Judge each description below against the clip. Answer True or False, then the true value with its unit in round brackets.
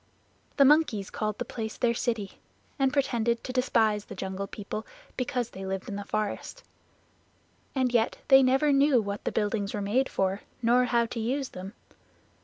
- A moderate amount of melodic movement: True (3.9 semitones)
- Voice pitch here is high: True (230 Hz)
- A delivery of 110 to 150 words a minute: False (175 wpm)